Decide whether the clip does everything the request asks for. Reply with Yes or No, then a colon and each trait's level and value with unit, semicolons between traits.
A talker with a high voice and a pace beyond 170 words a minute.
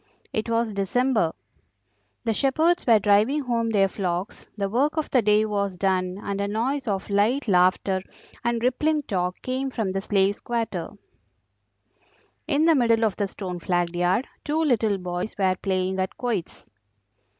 No: high, 210 Hz; average, 160 wpm